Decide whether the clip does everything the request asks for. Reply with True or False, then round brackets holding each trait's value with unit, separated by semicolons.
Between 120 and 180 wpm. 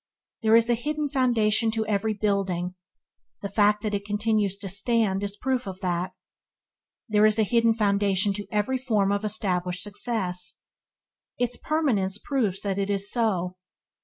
True (160 wpm)